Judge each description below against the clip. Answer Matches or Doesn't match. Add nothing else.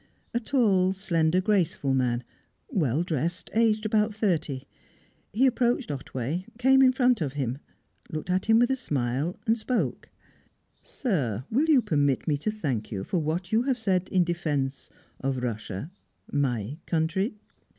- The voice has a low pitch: Doesn't match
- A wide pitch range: Matches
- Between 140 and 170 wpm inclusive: Matches